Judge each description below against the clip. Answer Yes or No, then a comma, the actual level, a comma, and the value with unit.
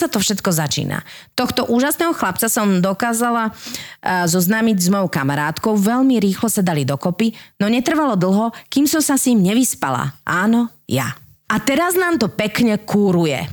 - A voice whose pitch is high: Yes, high, 220 Hz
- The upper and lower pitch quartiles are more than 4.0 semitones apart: Yes, average, 4.7 semitones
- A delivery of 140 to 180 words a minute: Yes, average, 150 wpm